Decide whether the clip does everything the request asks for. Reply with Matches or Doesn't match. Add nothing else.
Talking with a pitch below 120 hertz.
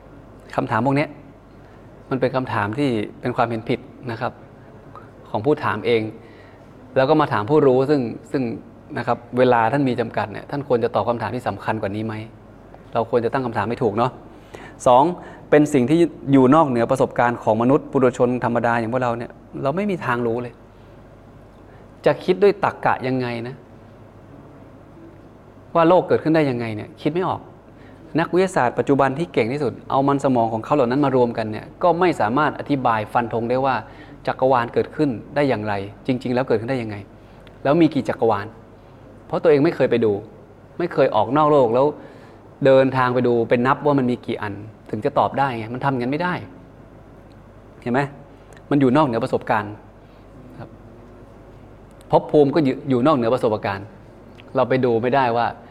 Doesn't match